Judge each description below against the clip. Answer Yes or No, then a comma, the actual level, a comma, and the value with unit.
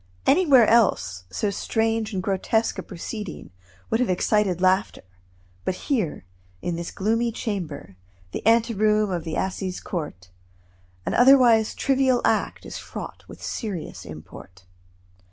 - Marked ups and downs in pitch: No, average, 4.6 semitones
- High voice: Yes, high, 210 Hz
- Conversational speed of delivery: No, slow, 130 wpm